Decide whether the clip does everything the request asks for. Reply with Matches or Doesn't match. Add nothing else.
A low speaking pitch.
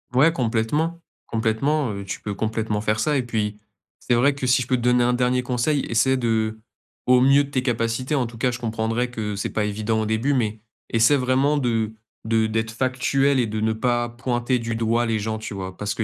Matches